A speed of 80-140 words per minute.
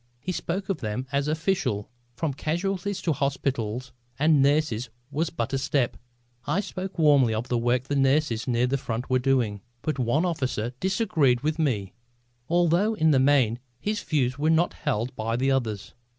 No: average, 175 wpm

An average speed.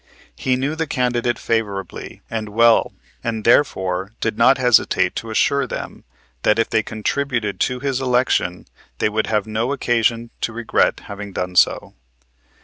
Yes: average, 150 wpm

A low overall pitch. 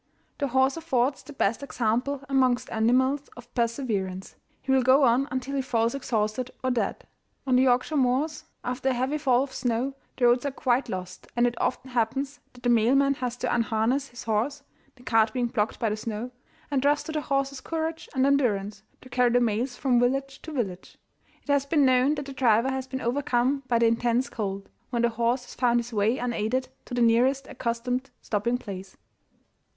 No: very high, 250 Hz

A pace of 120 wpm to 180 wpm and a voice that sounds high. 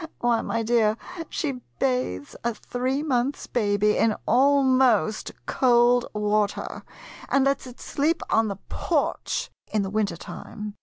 Yes: average, 140 wpm; high, 240 Hz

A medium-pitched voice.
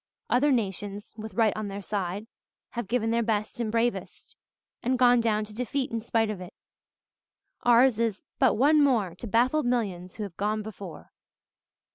No: high, 220 Hz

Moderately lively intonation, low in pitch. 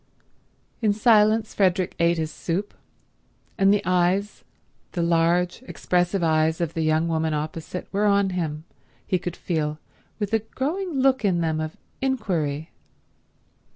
No: average, 4.3 semitones; medium, 180 Hz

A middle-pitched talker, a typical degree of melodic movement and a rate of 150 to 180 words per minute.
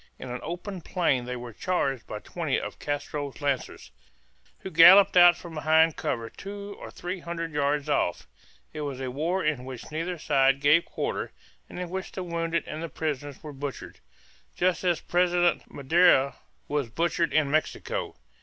Yes: medium, 155 Hz; average, 4.0 semitones; average, 170 wpm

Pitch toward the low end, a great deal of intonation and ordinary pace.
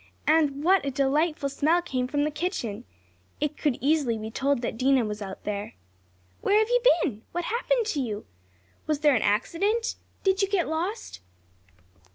No: very high, 295 Hz; wide, 5.9 semitones; average, 175 wpm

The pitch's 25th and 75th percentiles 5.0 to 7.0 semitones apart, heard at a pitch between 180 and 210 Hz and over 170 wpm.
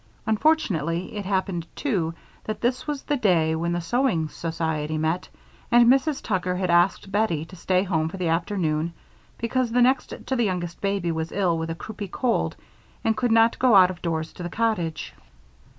Yes: wide, 5.4 semitones; medium, 185 Hz; average, 185 wpm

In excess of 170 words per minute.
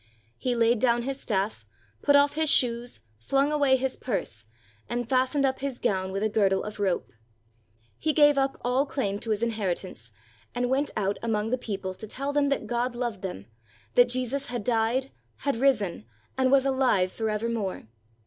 Yes: average, 180 wpm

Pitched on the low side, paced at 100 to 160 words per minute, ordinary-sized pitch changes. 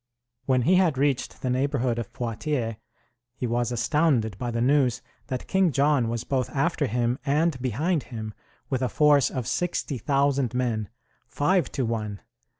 Yes: low, 130 Hz; average, 155 wpm; average, 3.6 semitones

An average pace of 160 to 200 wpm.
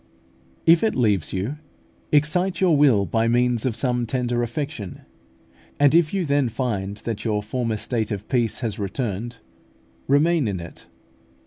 No: average, 150 wpm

